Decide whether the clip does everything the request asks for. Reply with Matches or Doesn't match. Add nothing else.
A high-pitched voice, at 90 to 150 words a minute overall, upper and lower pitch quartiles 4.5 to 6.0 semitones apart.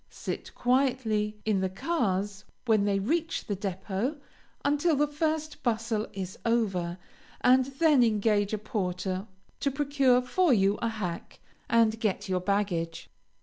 Matches